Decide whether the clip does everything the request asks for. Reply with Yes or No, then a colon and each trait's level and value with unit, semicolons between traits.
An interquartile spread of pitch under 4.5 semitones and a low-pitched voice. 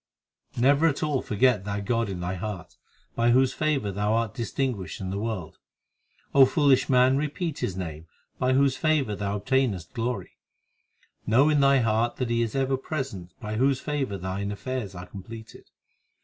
No: average, 5.0 semitones; low, 115 Hz